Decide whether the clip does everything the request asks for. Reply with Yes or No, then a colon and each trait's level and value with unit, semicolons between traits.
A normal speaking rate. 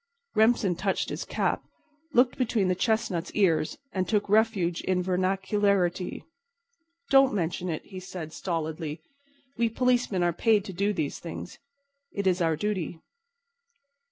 No: slow, 130 wpm